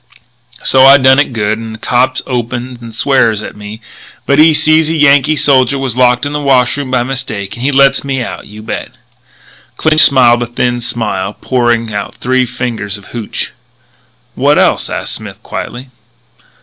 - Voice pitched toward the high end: No, low, 125 Hz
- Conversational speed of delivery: Yes, average, 180 wpm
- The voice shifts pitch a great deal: No, average, 3.1 semitones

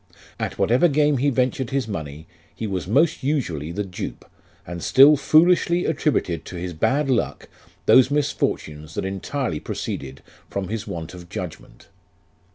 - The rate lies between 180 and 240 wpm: No, average, 150 wpm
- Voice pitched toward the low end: Yes, low, 115 Hz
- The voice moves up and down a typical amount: No, wide, 8.6 semitones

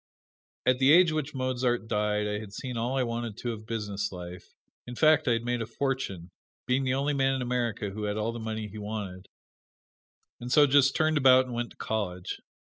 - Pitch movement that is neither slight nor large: Yes, average, 3.9 semitones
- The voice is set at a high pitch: No, low, 120 Hz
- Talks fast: Yes, fast, 210 wpm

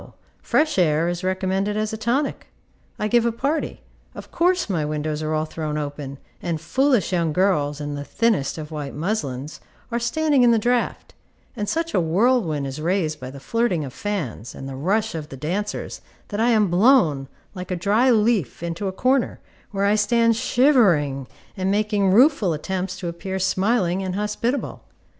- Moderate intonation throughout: No, wide, 6.8 semitones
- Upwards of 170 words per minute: Yes, average, 180 wpm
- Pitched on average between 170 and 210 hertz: Yes, high, 190 Hz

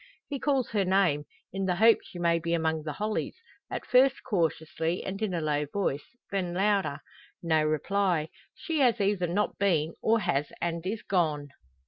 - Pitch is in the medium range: Yes, medium, 180 Hz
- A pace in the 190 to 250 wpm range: No, average, 175 wpm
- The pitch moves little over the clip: No, average, 4.3 semitones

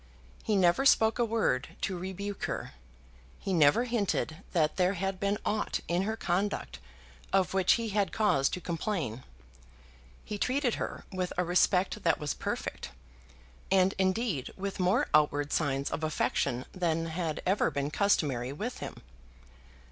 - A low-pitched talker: No, medium, 185 Hz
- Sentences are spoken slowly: No, average, 150 wpm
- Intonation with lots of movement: No, average, 4.6 semitones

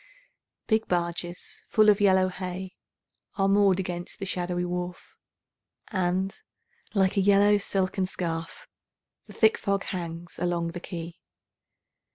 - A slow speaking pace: Yes, slow, 125 wpm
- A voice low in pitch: No, medium, 185 Hz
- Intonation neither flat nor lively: No, narrow, 2.0 semitones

